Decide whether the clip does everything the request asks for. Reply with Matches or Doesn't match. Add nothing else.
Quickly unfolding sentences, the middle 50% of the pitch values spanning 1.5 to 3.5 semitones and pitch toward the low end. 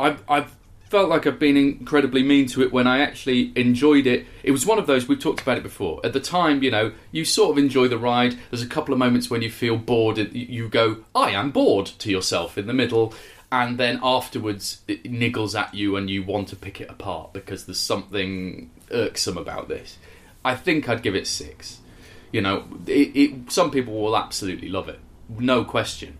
Doesn't match